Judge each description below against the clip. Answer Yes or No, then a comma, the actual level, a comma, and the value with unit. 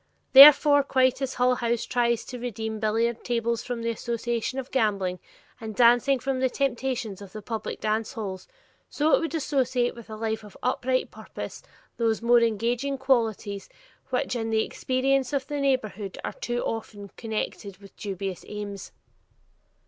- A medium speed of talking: Yes, average, 160 wpm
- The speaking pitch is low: No, high, 235 Hz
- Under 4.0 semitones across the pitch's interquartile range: Yes, average, 3.0 semitones